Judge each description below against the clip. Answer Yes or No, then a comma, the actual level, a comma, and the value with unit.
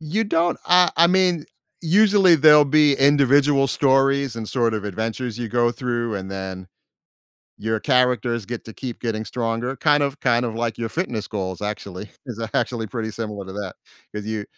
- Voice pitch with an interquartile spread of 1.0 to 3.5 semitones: No, average, 4.7 semitones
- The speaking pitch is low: Yes, low, 120 Hz